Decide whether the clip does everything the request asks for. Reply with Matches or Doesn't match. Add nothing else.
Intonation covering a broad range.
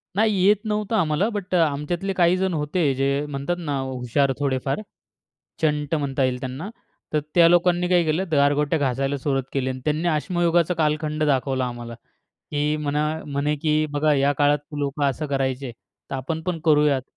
Doesn't match